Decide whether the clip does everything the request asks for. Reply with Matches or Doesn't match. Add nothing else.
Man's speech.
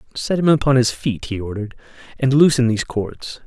Matches